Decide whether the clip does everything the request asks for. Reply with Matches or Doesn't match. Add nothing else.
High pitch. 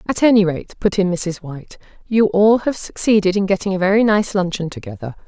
Matches